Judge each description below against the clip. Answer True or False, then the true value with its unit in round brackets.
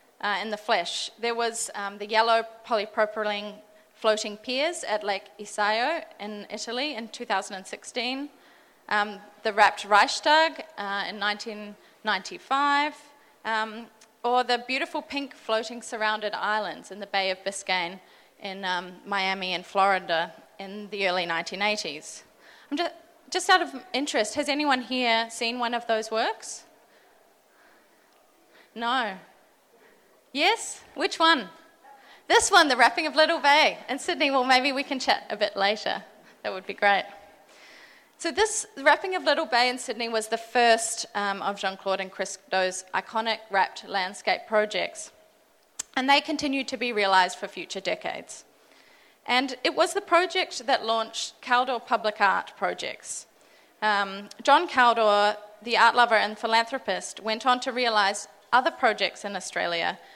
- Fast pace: False (145 wpm)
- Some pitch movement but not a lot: True (4.8 semitones)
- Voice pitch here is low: False (225 Hz)